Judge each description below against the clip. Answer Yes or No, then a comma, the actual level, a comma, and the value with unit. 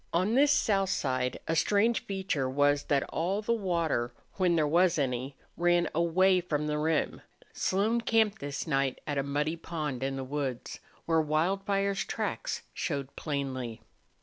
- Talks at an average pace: Yes, average, 155 wpm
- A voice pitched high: No, medium, 160 Hz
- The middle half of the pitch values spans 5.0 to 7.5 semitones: Yes, wide, 5.4 semitones